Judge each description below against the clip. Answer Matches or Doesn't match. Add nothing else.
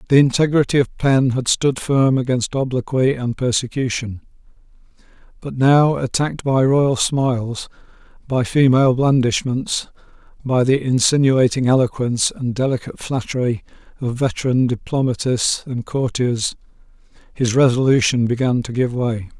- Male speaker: Matches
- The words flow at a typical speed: Doesn't match